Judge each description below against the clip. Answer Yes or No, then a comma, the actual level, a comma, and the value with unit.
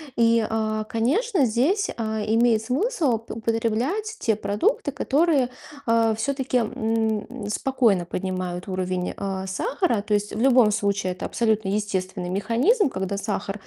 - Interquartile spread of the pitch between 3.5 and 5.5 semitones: Yes, average, 4.2 semitones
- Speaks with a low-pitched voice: No, high, 225 Hz